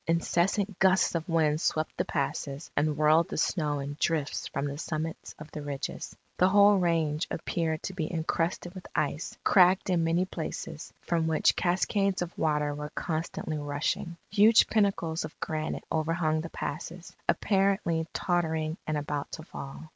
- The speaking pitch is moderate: Yes, medium, 160 Hz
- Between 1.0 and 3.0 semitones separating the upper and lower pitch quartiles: Yes, narrow, 2.6 semitones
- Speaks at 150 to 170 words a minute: Yes, average, 160 wpm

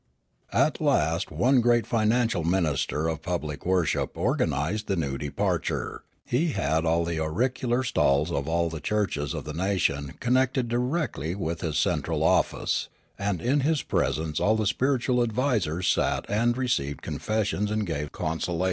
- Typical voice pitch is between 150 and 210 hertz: No, very low, 95 Hz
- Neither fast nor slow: Yes, average, 155 wpm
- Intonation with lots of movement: Yes, wide, 7.1 semitones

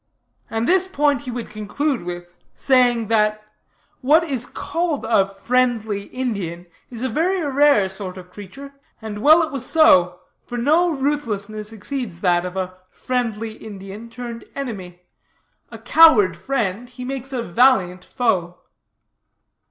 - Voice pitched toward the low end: No, high, 230 Hz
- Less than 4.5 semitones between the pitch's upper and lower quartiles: No, wide, 5.6 semitones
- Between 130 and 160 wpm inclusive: Yes, average, 140 wpm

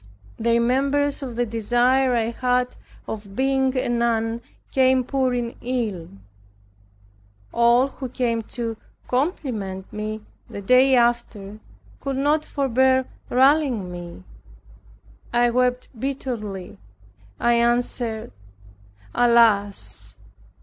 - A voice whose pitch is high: Yes, high, 240 Hz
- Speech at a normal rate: No, slow, 100 wpm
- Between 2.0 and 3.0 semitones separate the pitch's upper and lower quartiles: Yes, average, 2.7 semitones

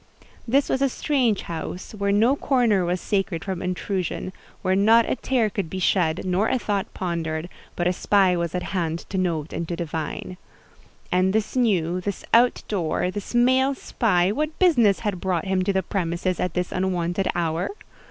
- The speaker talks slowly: No, average, 180 wpm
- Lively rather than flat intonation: No, average, 3.7 semitones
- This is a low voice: No, high, 190 Hz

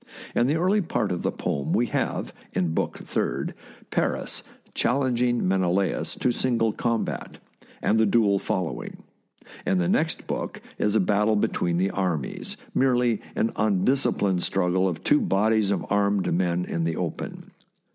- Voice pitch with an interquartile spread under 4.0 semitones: No, average, 4.4 semitones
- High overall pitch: No, low, 100 Hz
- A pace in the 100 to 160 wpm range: Yes, average, 155 wpm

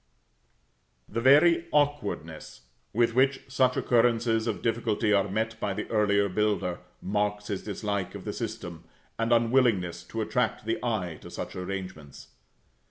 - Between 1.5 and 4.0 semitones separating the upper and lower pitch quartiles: Yes, average, 3.3 semitones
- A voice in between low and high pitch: No, low, 110 Hz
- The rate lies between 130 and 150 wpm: Yes, average, 140 wpm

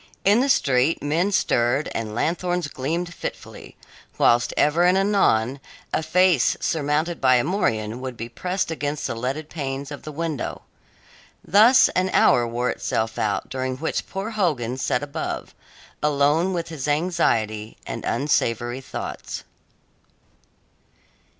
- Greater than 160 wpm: No, slow, 135 wpm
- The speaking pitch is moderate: Yes, medium, 145 Hz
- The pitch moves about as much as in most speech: No, wide, 5.8 semitones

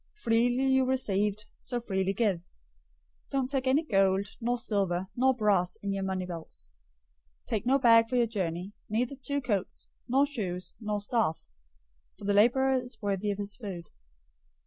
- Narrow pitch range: No, average, 4.4 semitones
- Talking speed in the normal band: Yes, average, 170 wpm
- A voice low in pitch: No, high, 215 Hz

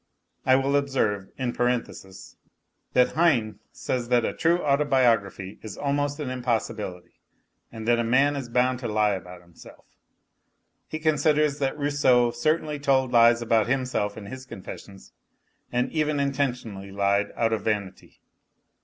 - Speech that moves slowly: No, average, 145 wpm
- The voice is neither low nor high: No, low, 125 Hz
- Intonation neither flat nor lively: Yes, average, 4.7 semitones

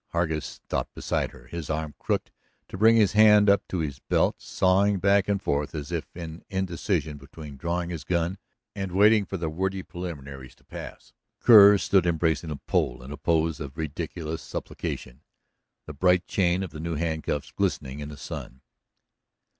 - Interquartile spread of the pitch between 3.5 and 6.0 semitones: Yes, average, 4.0 semitones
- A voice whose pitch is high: No, very low, 85 Hz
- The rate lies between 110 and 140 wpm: No, average, 175 wpm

